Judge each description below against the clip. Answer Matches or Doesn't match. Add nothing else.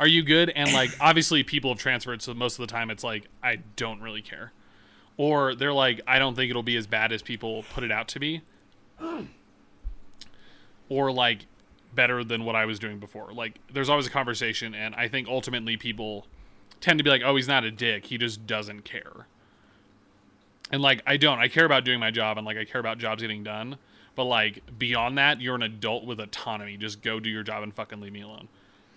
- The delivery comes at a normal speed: Doesn't match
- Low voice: Matches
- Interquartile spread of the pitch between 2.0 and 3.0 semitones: Doesn't match